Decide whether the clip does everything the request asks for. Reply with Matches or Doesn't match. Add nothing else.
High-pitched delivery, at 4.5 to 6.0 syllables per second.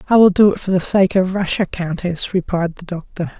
Doesn't match